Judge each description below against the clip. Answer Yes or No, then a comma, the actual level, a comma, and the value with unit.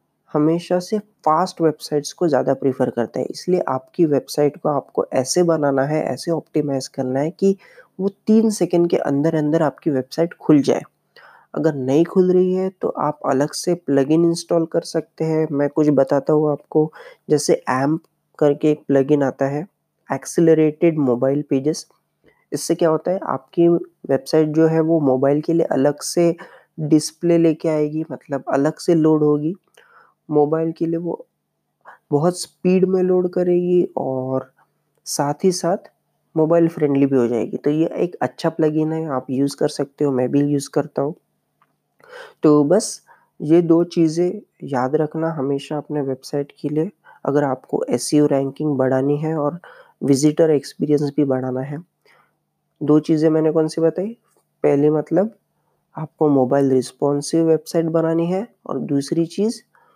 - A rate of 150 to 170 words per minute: Yes, average, 160 wpm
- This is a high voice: No, medium, 155 Hz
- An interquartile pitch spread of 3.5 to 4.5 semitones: No, average, 2.9 semitones